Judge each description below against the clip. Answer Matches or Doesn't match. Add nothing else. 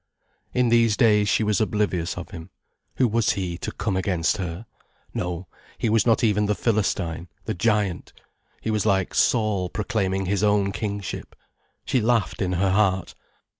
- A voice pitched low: Matches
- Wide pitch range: Doesn't match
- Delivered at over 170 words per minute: Doesn't match